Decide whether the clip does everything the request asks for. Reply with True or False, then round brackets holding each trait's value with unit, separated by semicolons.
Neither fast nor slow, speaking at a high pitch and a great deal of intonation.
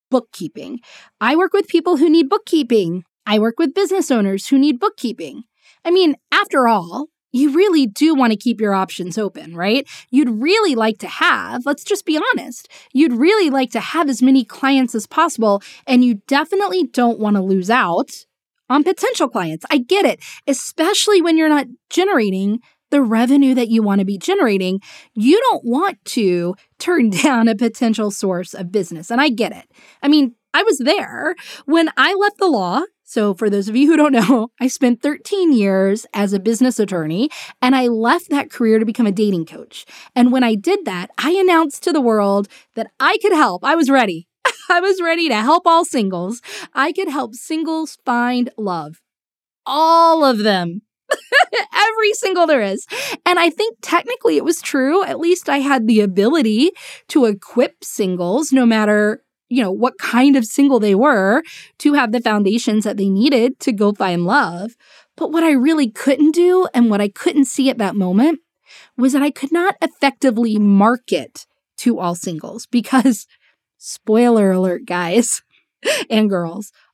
True (180 wpm; 260 Hz; 7.0 semitones)